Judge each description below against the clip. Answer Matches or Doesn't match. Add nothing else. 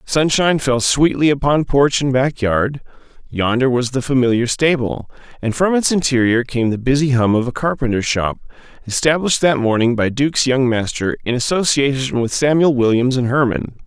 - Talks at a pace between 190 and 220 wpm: Doesn't match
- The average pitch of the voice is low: Matches